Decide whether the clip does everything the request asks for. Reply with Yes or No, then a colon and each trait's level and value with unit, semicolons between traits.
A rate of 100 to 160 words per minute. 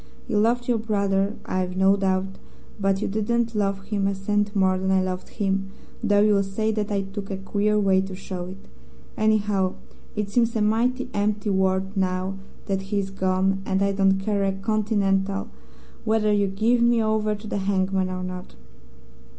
No: average, 185 wpm